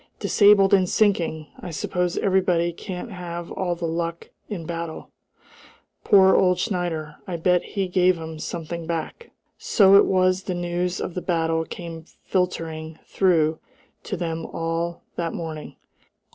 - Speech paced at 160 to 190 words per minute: No, average, 145 wpm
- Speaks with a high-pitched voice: No, medium, 175 Hz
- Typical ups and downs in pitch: No, narrow, 2.0 semitones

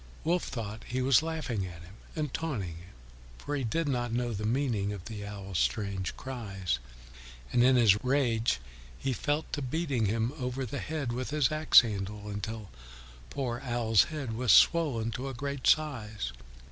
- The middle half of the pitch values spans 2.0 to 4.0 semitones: No, average, 4.9 semitones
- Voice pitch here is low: Yes, low, 120 Hz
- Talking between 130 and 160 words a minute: No, average, 170 wpm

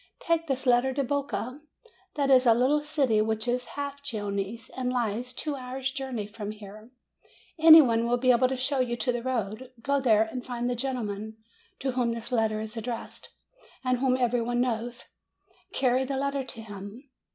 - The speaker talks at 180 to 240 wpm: Yes, average, 185 wpm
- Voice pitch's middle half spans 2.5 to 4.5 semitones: Yes, average, 2.8 semitones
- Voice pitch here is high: Yes, very high, 250 Hz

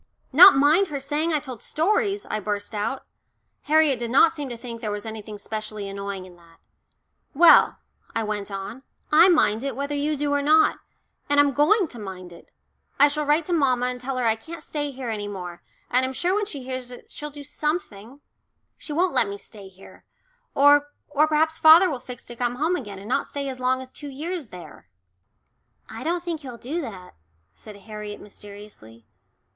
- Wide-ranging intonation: Yes, wide, 6.1 semitones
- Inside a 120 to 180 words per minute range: No, average, 200 wpm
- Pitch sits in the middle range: No, very high, 260 Hz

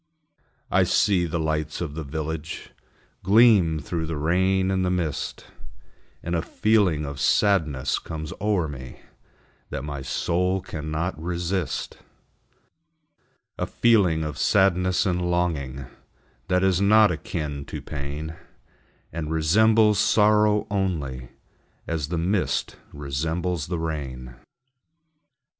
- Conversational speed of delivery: No, slow, 115 wpm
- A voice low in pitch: Yes, very low, 85 Hz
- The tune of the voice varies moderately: Yes, average, 3.8 semitones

